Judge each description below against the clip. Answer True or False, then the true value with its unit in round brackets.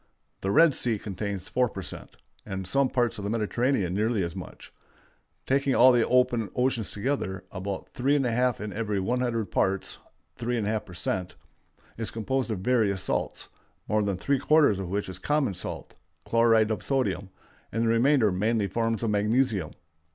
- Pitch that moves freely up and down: False (4.2 semitones)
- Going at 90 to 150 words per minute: False (165 wpm)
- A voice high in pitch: False (110 Hz)